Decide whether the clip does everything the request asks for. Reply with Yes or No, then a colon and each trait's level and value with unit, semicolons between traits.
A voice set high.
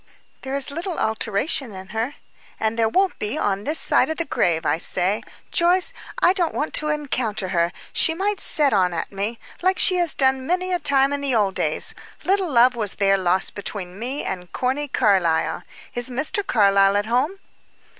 Yes: high, 245 Hz